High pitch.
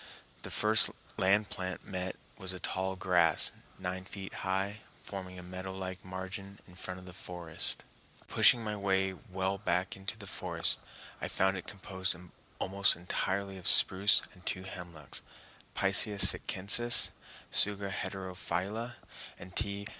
No: very low, 95 Hz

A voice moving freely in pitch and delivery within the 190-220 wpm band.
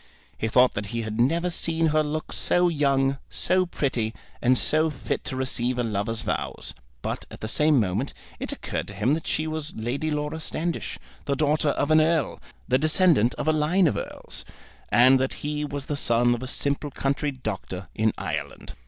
No: average, 4.8 semitones; average, 195 wpm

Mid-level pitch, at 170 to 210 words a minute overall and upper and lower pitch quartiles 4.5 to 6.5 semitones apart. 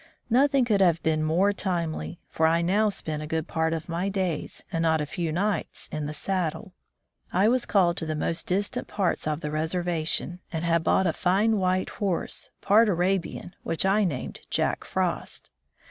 No: medium, 175 Hz; average, 185 wpm; average, 3.3 semitones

